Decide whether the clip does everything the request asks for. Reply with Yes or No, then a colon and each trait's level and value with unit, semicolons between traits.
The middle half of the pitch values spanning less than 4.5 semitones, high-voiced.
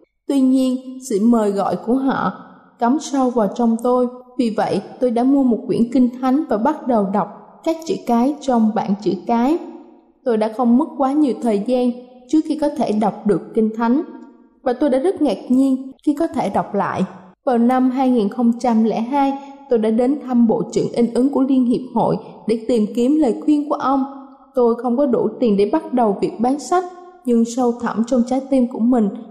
Yes: average, 3.1 semitones; very high, 250 Hz